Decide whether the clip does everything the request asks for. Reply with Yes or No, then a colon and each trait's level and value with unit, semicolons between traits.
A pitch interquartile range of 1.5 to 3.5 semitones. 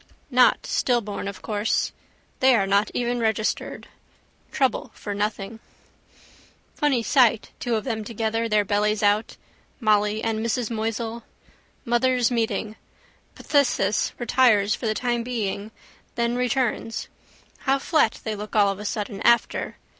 Yes: narrow, 2.4 semitones